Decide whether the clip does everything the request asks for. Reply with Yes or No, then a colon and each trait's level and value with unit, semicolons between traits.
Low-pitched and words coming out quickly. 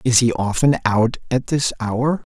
No: low, 125 Hz; average, 180 wpm